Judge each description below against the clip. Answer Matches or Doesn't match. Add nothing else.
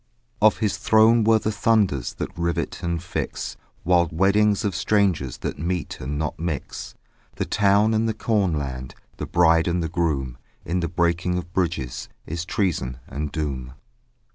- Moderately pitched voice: Doesn't match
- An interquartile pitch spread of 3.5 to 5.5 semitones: Matches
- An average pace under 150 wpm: Doesn't match